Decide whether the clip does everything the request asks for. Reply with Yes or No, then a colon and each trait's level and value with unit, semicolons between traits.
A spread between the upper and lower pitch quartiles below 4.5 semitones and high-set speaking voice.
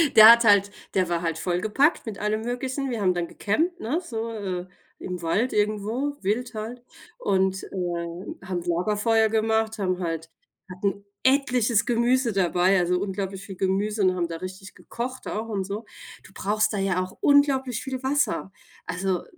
Yes: average, 4.1 semitones; high, 205 Hz